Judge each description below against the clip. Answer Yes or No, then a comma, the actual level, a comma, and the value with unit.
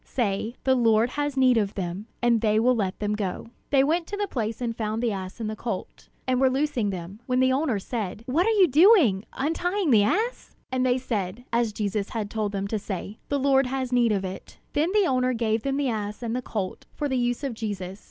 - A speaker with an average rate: No, fast, 235 wpm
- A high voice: Yes, high, 235 Hz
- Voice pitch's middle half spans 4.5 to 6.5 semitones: No, average, 4.1 semitones